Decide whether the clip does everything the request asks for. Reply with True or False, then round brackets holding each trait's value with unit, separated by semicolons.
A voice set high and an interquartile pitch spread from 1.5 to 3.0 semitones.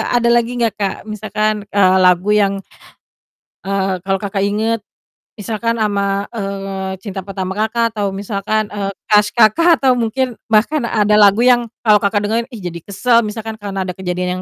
True (205 Hz; 2.6 semitones)